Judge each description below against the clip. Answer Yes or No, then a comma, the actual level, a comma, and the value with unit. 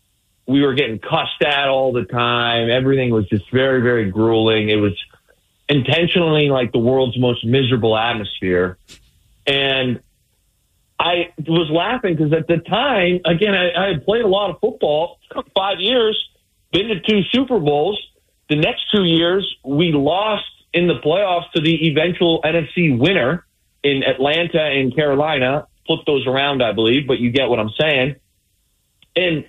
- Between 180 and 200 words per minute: No, average, 155 wpm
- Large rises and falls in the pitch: Yes, wide, 5.8 semitones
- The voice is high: No, medium, 145 Hz